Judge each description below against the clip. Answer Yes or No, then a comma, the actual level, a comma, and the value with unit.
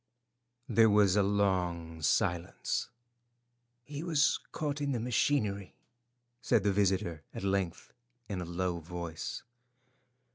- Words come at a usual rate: No, slow, 115 wpm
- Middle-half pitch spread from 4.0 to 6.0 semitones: Yes, average, 4.5 semitones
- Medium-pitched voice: No, low, 100 Hz